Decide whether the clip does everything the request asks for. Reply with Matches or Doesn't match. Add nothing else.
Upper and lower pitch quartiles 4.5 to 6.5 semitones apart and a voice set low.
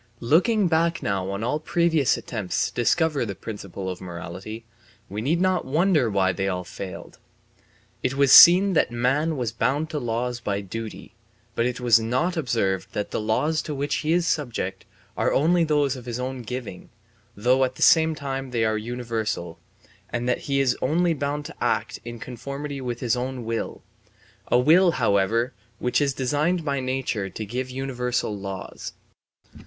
Matches